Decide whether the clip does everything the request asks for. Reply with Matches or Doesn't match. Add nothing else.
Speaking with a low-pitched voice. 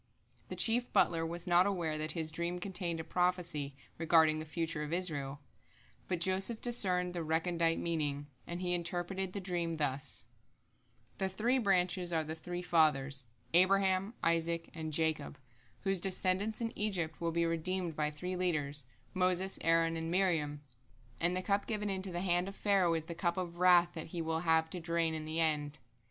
Doesn't match